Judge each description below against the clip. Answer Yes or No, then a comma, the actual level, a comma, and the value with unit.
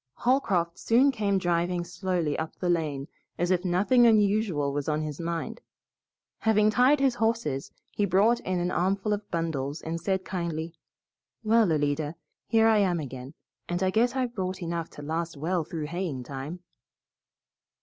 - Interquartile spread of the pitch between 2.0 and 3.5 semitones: No, average, 4.9 semitones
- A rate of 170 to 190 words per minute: No, average, 160 wpm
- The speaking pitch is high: No, medium, 175 Hz